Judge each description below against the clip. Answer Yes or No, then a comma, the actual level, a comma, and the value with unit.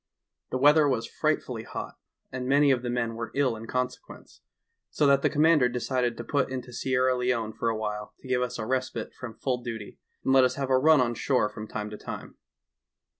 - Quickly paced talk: Yes, fast, 215 wpm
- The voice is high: No, low, 125 Hz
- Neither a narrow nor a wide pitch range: No, narrow, 2.3 semitones